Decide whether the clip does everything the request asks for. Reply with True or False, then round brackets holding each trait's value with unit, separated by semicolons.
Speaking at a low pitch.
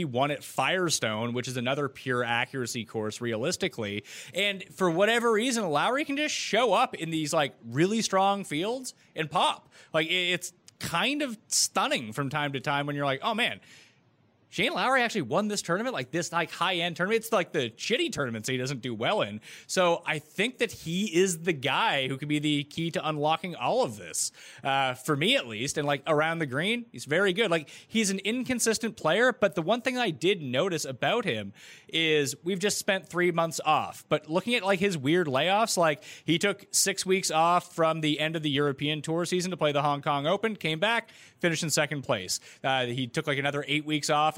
False (160 Hz)